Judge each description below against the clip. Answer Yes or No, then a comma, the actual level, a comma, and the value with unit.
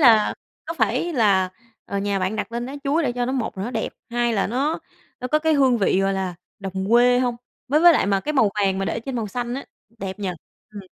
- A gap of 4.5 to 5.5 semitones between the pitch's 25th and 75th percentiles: Yes, average, 4.8 semitones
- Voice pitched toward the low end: No, high, 235 Hz